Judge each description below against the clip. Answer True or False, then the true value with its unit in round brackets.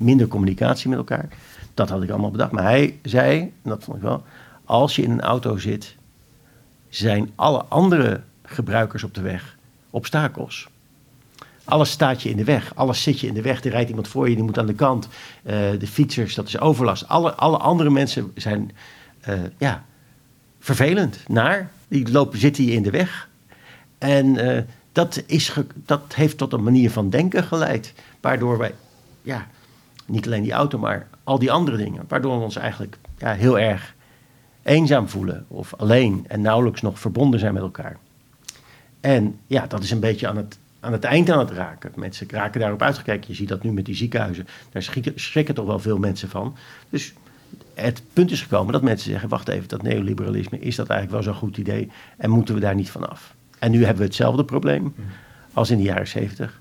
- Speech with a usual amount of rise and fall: True (4.3 semitones)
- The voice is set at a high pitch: False (120 Hz)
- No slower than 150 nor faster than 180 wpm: False (195 wpm)